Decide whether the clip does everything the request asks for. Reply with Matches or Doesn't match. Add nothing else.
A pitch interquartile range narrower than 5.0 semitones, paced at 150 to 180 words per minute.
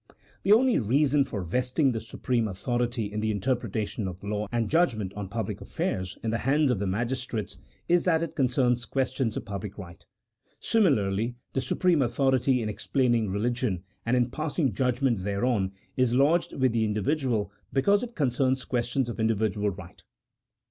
Matches